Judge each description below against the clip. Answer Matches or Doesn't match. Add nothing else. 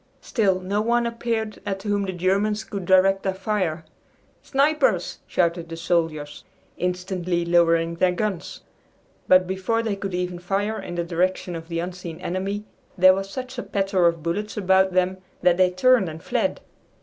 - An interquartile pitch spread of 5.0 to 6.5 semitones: Doesn't match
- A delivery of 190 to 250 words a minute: Doesn't match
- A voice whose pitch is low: Doesn't match